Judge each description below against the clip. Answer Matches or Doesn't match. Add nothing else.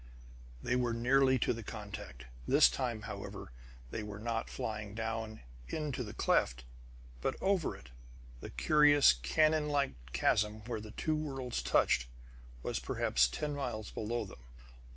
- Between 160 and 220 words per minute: Doesn't match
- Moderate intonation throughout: Matches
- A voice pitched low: Matches